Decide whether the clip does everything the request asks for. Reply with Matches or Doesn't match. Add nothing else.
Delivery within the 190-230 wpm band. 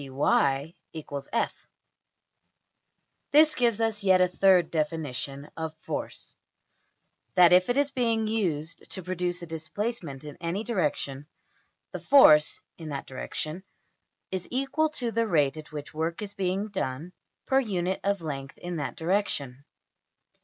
Doesn't match